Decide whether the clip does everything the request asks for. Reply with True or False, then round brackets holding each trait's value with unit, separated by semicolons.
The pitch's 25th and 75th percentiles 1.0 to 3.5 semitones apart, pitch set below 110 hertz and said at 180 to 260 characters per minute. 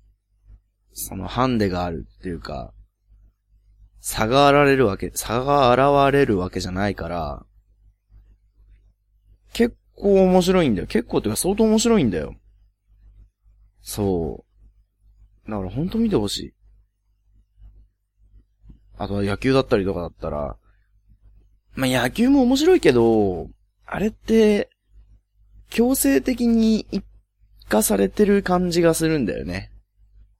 False (5.3 semitones; 100 Hz; 230 characters per minute)